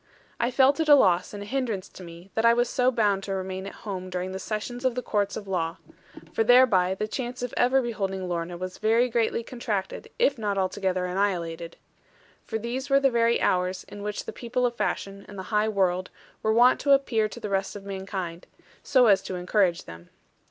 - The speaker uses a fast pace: Yes, fast, 215 wpm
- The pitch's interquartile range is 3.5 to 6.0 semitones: Yes, average, 4.3 semitones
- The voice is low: No, high, 205 Hz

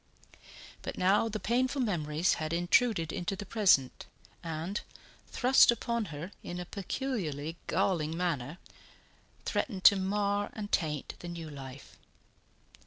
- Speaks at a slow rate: Yes, slow, 125 wpm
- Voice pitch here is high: No, medium, 180 Hz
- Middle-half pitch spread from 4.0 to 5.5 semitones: Yes, average, 4.8 semitones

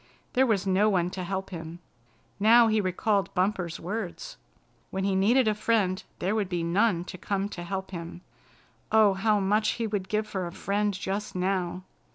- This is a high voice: Yes, high, 195 Hz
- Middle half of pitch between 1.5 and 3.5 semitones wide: Yes, narrow, 2.6 semitones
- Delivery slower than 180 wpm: No, average, 185 wpm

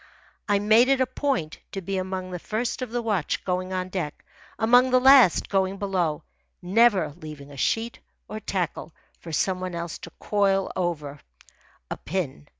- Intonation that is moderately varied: Yes, average, 4.4 semitones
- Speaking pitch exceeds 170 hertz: Yes, high, 190 Hz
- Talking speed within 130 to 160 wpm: No, average, 170 wpm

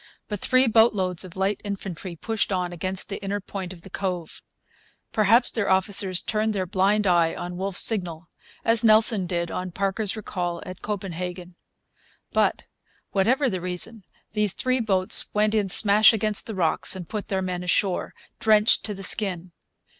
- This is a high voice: Yes, high, 195 Hz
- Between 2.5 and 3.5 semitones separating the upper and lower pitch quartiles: Yes, average, 2.8 semitones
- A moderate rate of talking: Yes, average, 165 wpm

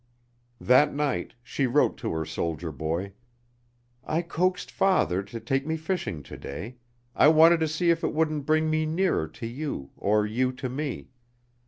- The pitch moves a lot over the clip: Yes, wide, 7.1 semitones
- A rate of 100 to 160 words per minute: No, average, 170 wpm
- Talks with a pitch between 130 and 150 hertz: Yes, medium, 140 Hz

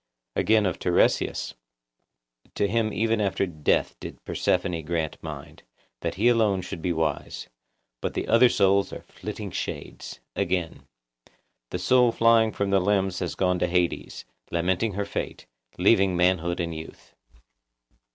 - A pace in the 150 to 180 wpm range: No, average, 140 wpm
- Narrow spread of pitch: No, average, 3.6 semitones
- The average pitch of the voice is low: Yes, very low, 95 Hz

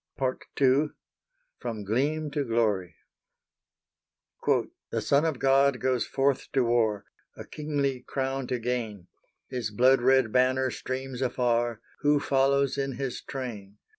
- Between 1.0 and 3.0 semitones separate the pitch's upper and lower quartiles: Yes, narrow, 2.5 semitones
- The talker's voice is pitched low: Yes, low, 130 Hz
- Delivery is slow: Yes, slow, 130 wpm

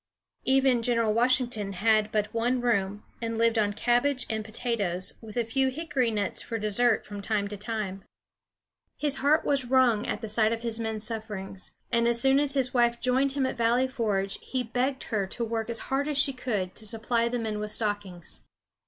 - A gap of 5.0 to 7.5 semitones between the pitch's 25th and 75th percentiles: No, average, 3.0 semitones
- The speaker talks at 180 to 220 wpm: Yes, average, 195 wpm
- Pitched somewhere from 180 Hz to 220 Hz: No, high, 230 Hz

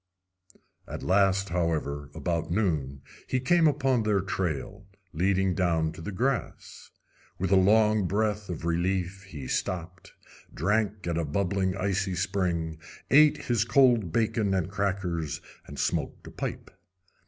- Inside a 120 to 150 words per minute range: Yes, slow, 135 wpm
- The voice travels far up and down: No, average, 3.7 semitones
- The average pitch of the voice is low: Yes, very low, 95 Hz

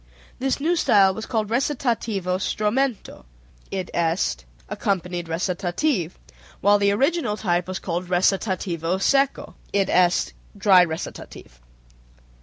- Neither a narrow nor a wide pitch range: Yes, average, 3.9 semitones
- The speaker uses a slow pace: Yes, slow, 100 wpm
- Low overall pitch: No, high, 195 Hz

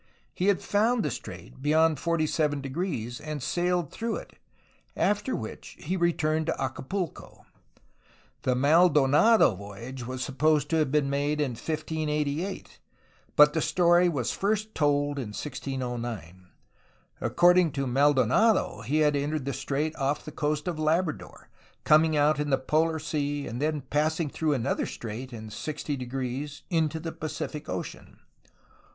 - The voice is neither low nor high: Yes, medium, 150 Hz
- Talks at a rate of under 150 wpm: Yes, average, 140 wpm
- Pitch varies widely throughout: No, average, 3.2 semitones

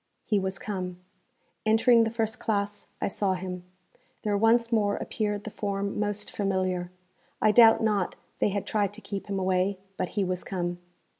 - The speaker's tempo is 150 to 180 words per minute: Yes, average, 170 wpm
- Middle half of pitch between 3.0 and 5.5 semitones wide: No, narrow, 2.4 semitones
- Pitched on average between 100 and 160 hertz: No, high, 200 Hz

